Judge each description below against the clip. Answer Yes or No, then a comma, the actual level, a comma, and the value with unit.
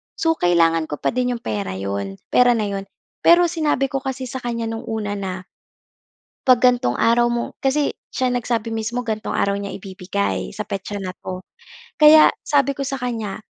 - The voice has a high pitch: Yes, high, 230 Hz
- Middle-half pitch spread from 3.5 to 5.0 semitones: Yes, average, 4.6 semitones